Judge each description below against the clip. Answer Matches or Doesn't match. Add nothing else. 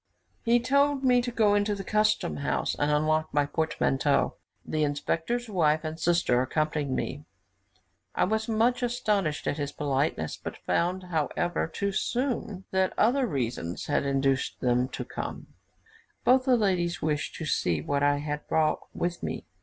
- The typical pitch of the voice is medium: Matches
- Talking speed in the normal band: Matches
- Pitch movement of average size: Doesn't match